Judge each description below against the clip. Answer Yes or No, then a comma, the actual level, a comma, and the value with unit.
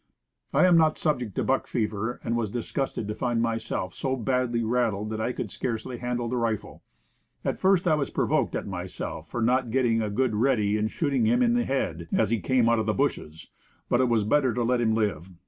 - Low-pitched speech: Yes, low, 120 Hz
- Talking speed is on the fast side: Yes, fast, 230 wpm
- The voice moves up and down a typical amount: Yes, average, 3.1 semitones